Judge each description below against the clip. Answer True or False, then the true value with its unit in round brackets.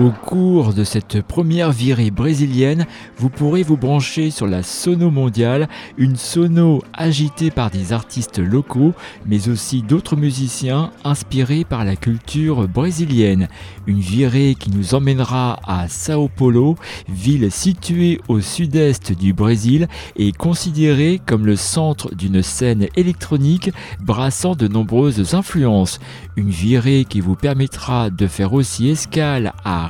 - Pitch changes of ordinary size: False (6.5 semitones)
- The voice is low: True (130 Hz)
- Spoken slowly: True (135 wpm)